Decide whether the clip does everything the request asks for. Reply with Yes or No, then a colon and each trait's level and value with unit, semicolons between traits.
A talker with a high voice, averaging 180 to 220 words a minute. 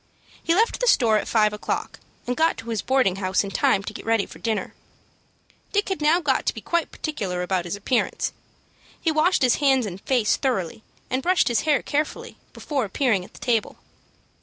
Yes: high, 245 Hz; average, 200 wpm